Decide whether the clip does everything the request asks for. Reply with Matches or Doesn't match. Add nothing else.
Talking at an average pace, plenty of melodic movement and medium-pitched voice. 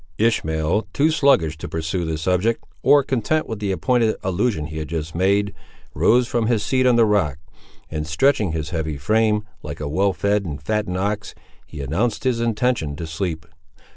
Doesn't match